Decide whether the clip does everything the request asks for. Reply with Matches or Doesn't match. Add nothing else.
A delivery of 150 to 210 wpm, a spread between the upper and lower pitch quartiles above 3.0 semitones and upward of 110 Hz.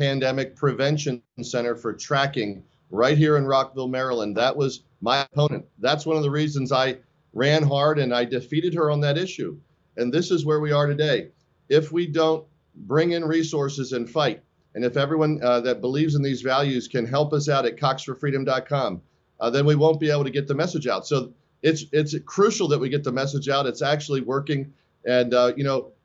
Doesn't match